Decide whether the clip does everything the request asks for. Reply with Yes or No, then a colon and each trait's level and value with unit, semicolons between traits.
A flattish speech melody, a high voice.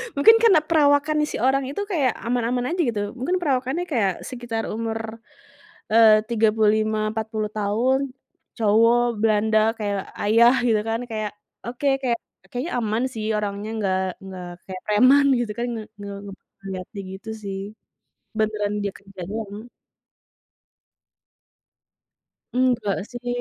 No: average, 3.2 semitones; high, 225 Hz